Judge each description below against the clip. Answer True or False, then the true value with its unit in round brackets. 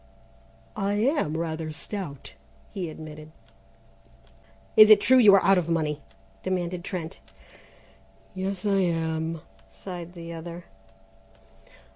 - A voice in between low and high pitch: True (175 Hz)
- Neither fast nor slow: False (110 wpm)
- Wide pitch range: False (3.4 semitones)